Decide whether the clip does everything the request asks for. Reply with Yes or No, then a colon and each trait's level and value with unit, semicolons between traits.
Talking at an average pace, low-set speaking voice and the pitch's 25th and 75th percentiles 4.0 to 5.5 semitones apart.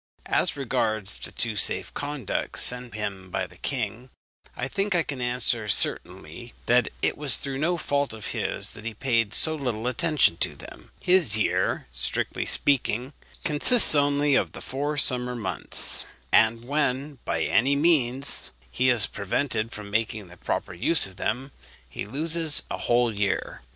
Yes: average, 160 wpm; low, 125 Hz; average, 4.8 semitones